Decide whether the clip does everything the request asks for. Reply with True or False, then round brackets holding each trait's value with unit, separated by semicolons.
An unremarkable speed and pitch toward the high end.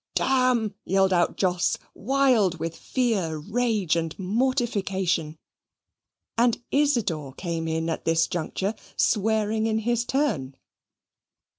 False (115 wpm; 200 Hz)